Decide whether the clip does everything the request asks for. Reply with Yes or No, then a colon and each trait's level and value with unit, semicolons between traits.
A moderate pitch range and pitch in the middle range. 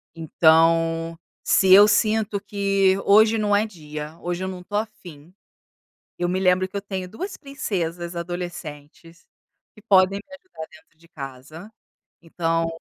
Yes: average, 3.6 semitones; medium, 180 Hz